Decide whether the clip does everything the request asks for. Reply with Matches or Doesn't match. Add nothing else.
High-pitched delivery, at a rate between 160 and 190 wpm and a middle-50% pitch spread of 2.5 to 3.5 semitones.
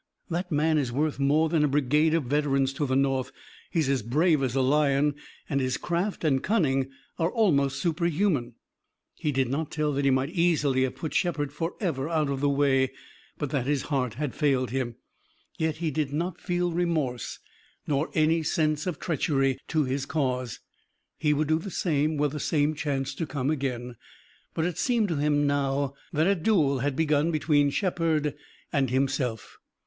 Doesn't match